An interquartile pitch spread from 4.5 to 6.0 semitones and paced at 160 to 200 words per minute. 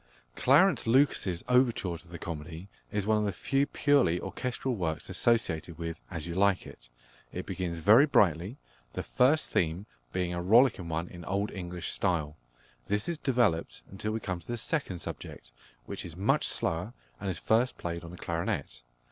Yes: average, 5.2 semitones; average, 175 wpm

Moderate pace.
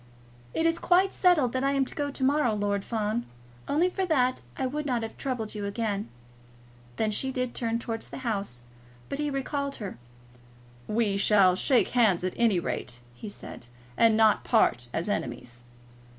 Yes: average, 180 wpm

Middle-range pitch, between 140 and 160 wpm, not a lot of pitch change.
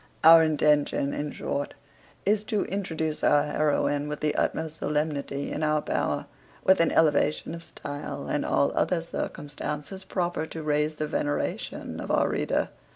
Yes: medium, 150 Hz; average, 155 wpm; narrow, 1.8 semitones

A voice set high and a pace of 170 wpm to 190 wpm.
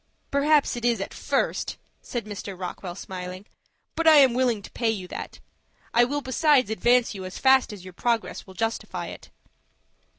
Yes: high, 230 Hz; average, 175 wpm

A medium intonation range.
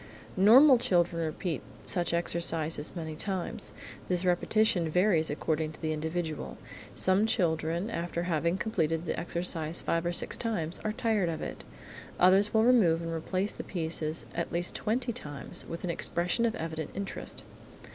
Yes: average, 3.5 semitones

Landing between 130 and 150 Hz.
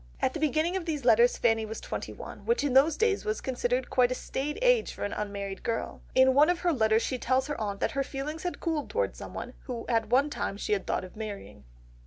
No: very high, 260 Hz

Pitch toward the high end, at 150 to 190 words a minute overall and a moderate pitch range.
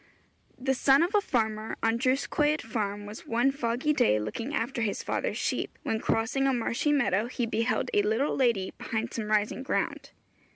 Yes: high, 230 Hz; average, 180 wpm; average, 3.7 semitones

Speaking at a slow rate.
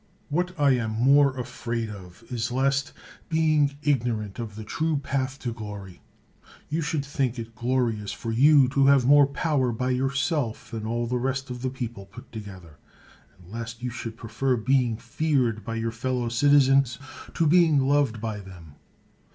No: average, 175 wpm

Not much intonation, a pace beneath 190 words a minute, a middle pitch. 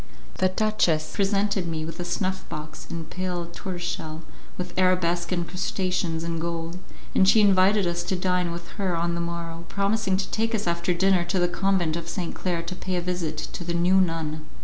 No: narrow, 1.9 semitones; average, 195 wpm; medium, 175 Hz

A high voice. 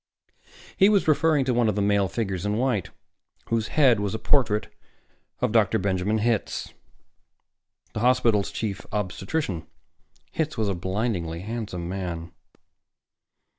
No: low, 105 Hz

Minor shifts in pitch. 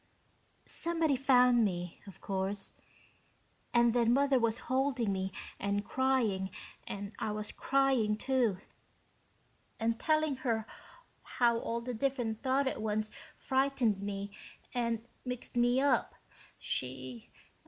No: average, 4.2 semitones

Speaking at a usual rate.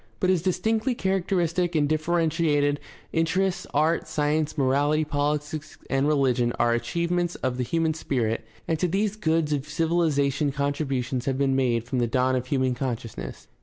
Yes: average, 160 wpm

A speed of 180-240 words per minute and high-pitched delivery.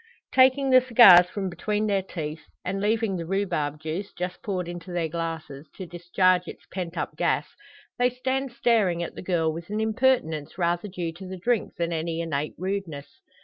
No: average, 185 wpm; medium, 180 Hz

